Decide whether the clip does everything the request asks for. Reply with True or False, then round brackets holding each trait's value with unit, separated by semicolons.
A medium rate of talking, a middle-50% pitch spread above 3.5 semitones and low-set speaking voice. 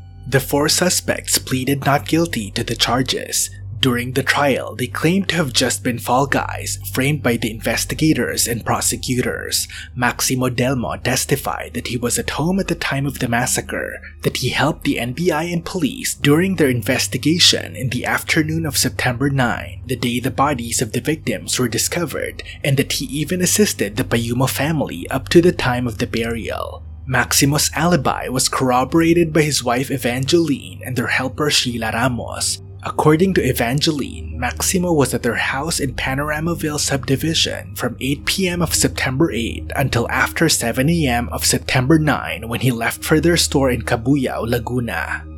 True (165 wpm; 4.2 semitones; 130 Hz)